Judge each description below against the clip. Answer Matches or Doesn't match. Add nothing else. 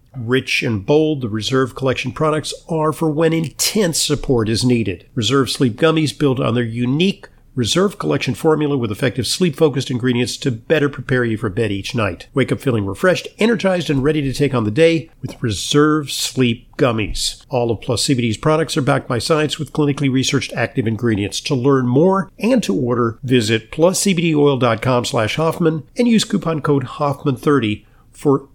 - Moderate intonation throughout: Matches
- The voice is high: Doesn't match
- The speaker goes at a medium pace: Matches